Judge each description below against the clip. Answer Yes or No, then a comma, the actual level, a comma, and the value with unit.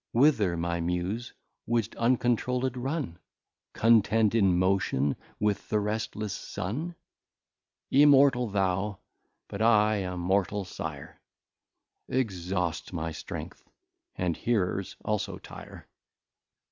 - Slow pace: Yes, slow, 95 wpm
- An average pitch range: Yes, average, 4.3 semitones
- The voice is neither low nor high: No, low, 105 Hz